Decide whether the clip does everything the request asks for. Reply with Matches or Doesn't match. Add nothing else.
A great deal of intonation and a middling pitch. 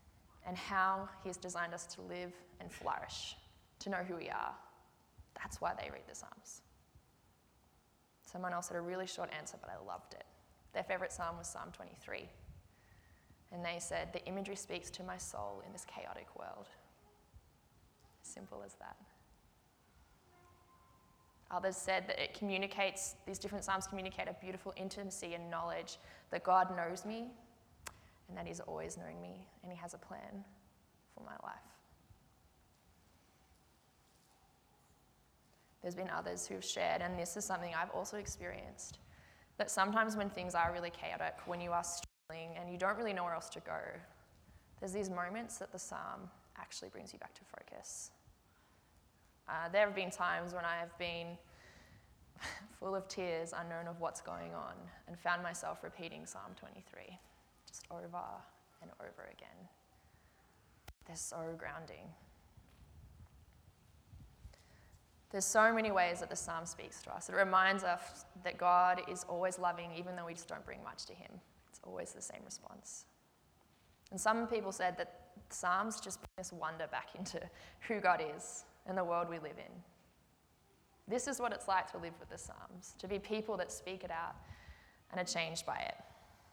Matches